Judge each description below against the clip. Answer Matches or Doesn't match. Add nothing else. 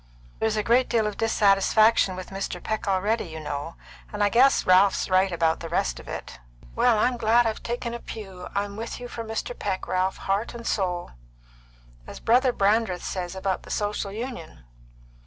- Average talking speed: Matches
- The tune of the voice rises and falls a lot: Doesn't match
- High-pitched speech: Matches